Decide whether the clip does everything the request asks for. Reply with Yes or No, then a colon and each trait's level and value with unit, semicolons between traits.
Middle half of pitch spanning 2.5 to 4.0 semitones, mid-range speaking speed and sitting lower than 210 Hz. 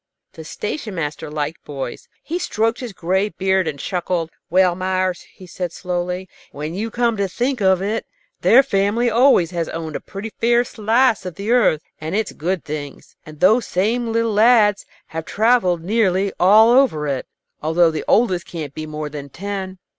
No: average, 5.2 semitones; average, 175 wpm; high, 190 Hz